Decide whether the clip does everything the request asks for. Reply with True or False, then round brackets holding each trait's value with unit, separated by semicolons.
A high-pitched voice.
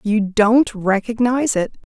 True (220 Hz)